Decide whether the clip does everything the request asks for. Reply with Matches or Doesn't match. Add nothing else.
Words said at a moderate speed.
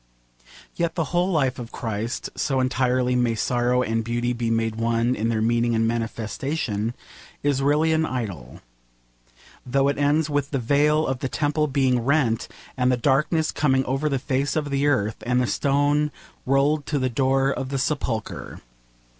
Matches